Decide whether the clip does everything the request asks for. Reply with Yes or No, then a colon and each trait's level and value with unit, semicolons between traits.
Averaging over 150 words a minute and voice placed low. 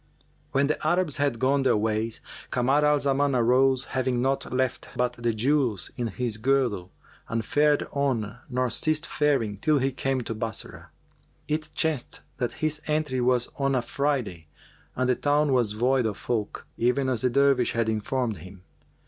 Yes: average, 170 wpm; low, 130 Hz